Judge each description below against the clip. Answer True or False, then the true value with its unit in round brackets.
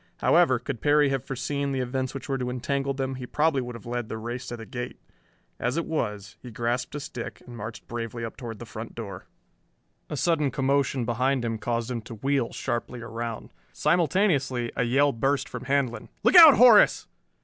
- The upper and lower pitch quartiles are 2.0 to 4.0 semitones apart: True (2.9 semitones)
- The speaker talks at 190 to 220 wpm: True (195 wpm)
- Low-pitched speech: True (125 Hz)